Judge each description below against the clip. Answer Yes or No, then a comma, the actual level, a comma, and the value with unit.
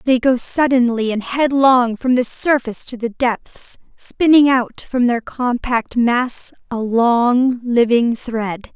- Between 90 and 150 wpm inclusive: Yes, average, 145 wpm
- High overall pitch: Yes, high, 245 Hz